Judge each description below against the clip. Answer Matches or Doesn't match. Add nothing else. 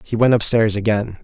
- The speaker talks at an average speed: Doesn't match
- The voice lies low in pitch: Matches